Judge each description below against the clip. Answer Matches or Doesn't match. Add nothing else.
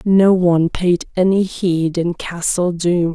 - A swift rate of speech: Doesn't match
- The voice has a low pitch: Doesn't match